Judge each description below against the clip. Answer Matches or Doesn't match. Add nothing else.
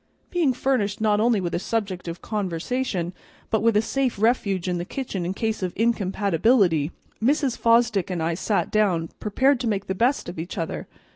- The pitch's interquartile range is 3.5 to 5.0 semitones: Matches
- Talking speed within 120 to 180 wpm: Doesn't match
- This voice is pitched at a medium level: Doesn't match